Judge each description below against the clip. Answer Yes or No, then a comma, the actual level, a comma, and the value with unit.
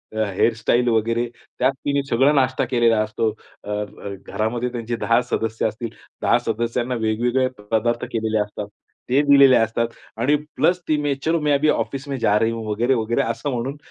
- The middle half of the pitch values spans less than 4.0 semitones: Yes, average, 2.9 semitones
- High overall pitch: No, low, 120 Hz